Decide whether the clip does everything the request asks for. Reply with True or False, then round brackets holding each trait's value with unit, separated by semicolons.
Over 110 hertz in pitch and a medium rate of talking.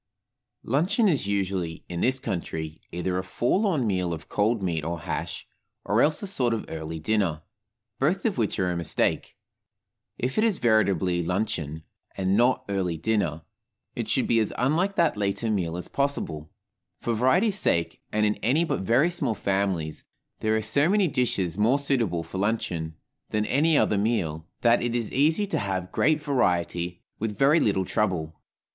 False (105 Hz; 170 wpm)